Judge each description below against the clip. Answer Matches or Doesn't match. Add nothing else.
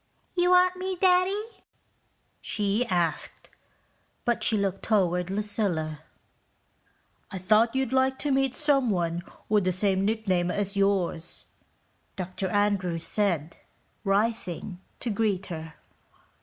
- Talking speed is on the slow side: Matches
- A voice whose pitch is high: Matches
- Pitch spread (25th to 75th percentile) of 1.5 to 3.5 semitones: Doesn't match